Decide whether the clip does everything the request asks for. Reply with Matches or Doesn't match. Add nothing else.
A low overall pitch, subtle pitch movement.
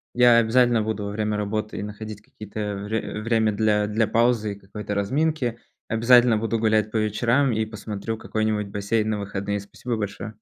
Matches